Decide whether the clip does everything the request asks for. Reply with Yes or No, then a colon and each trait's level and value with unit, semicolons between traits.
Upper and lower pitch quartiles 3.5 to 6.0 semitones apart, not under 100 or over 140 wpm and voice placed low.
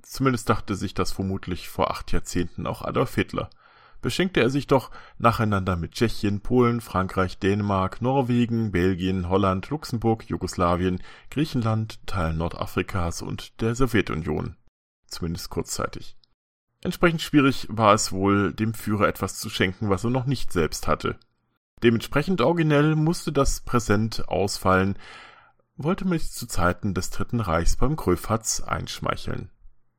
Yes: average, 4.8 semitones; average, 135 wpm; low, 110 Hz